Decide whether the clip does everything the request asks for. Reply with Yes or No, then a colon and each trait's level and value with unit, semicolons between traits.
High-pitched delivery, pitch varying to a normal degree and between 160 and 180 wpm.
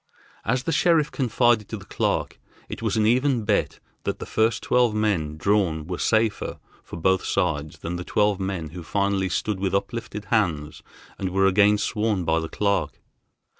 No: low, 100 Hz; average, 3.5 semitones; average, 175 wpm